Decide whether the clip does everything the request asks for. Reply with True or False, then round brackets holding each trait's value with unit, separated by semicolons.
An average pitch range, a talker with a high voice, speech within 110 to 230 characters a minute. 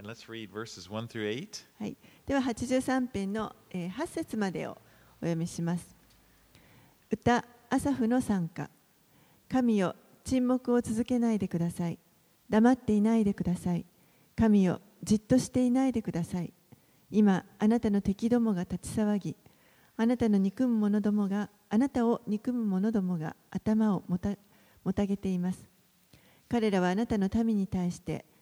True (4.7 semitones; 205 Hz; 225 characters per minute)